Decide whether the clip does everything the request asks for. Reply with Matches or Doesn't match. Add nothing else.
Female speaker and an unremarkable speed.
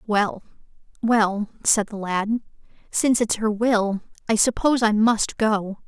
Matches